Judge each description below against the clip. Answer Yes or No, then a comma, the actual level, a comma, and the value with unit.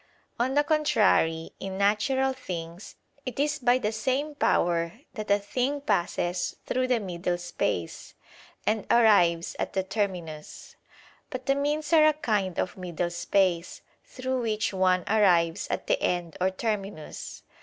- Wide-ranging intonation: Yes, wide, 6.6 semitones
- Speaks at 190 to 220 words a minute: No, average, 145 wpm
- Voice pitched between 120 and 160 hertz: No, high, 205 Hz